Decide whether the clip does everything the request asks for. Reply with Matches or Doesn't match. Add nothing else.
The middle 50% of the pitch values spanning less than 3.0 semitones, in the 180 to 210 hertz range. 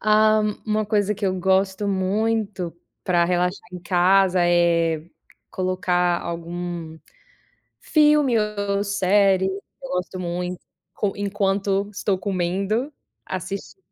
Matches